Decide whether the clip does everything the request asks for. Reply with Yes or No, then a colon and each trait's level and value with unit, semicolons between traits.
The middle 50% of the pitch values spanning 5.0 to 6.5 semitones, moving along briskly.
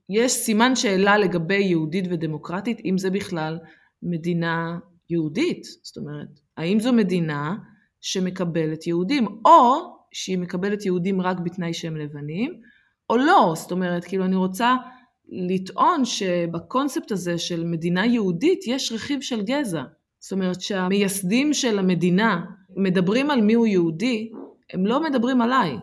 No: average, 5.3 semitones; average, 130 wpm